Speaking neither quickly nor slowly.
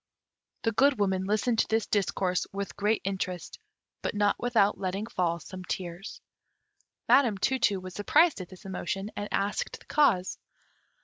Yes: average, 160 wpm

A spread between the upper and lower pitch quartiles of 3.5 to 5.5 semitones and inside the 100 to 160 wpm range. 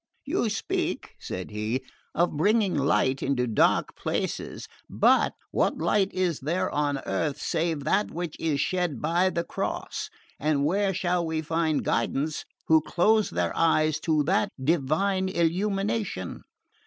Yes: average, 4.2 semitones; average, 140 wpm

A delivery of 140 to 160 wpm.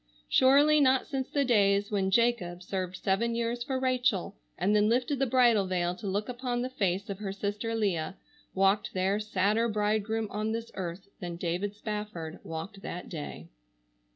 No: average, 170 wpm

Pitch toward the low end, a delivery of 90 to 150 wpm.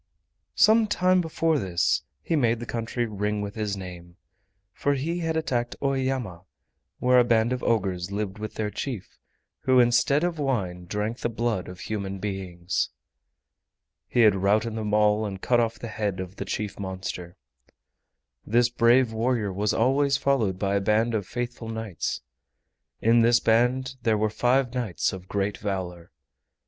No: low, 110 Hz; average, 160 wpm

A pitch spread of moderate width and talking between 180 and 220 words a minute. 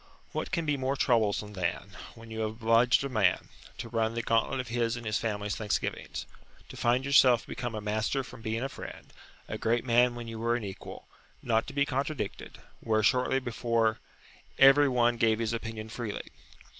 No: narrow, 2.2 semitones; average, 190 wpm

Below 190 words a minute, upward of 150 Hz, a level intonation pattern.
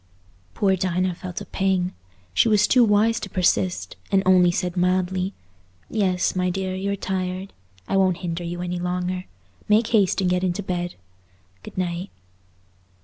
Yes: average, 155 wpm; medium, 185 Hz; narrow, 1.3 semitones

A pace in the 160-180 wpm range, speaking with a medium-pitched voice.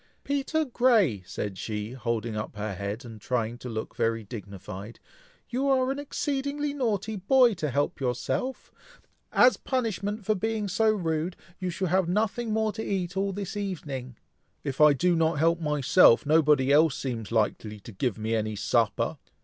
Yes: average, 170 wpm; medium, 160 Hz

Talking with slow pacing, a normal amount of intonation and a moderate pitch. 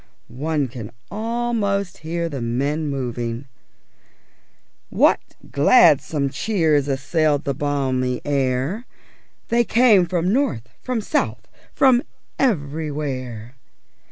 No: slow, 100 wpm; wide, 6.9 semitones; medium, 150 Hz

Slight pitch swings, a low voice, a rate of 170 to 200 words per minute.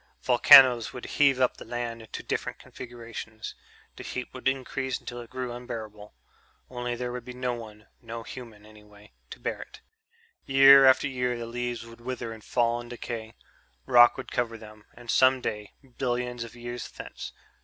Yes: narrow, 1.6 semitones; low, 120 Hz; average, 175 wpm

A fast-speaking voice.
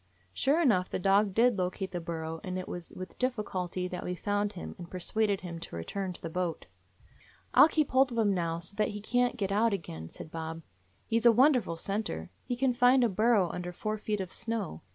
Yes: fast, 230 wpm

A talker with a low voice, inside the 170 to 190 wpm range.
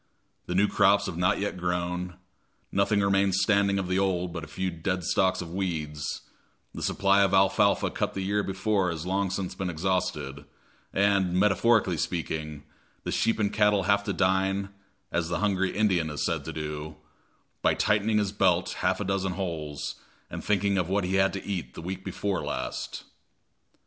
Yes: very low, 95 Hz; average, 175 wpm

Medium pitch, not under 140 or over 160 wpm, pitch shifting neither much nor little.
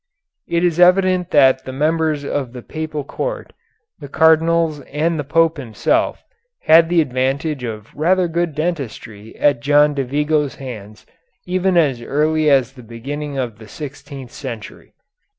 Yes: medium, 145 Hz; average, 150 wpm; average, 3.7 semitones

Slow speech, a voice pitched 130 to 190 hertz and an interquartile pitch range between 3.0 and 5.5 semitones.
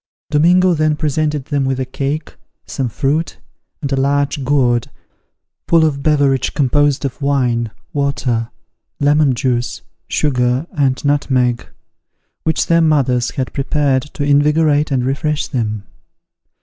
No: slow, 125 wpm; medium, 140 Hz; narrow, 2.6 semitones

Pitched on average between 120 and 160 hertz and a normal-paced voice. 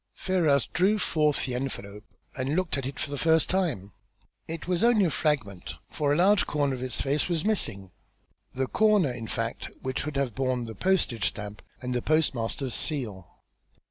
Yes: medium, 140 Hz; average, 180 wpm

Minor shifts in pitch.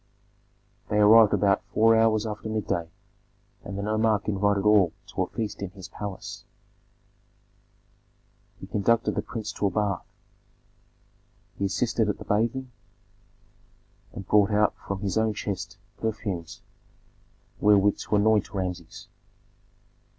Yes: narrow, 1.7 semitones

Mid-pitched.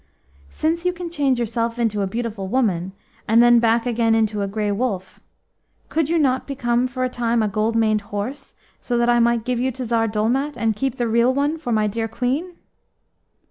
No: high, 235 Hz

